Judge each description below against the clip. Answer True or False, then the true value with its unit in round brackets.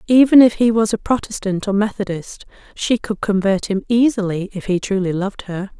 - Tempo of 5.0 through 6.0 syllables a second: True (5.4 syllables/s)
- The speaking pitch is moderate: False (205 Hz)